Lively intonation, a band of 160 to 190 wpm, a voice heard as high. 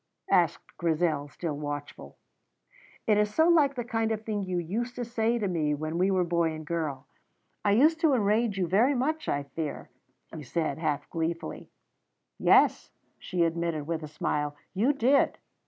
No: wide, 6.5 semitones; average, 170 wpm; medium, 180 Hz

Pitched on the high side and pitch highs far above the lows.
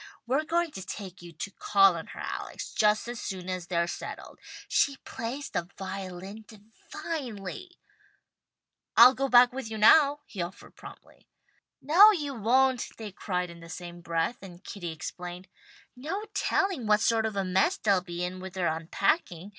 Yes: high, 205 Hz; wide, 6.3 semitones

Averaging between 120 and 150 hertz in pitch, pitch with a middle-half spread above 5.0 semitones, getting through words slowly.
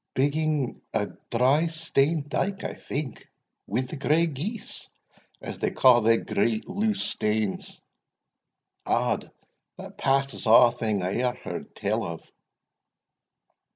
Yes: low, 135 Hz; wide, 5.5 semitones; slow, 120 wpm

